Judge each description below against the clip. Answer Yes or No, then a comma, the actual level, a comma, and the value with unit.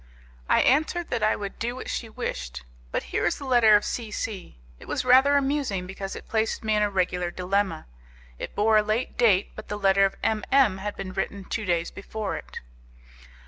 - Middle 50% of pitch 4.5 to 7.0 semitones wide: No, average, 3.4 semitones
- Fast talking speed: Yes, fast, 210 wpm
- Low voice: No, high, 210 Hz